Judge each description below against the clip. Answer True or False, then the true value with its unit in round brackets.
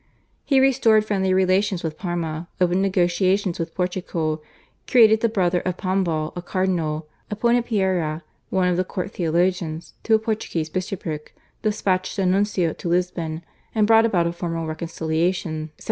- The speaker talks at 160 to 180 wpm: False (150 wpm)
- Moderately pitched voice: True (180 Hz)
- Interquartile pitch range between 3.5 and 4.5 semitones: False (2.9 semitones)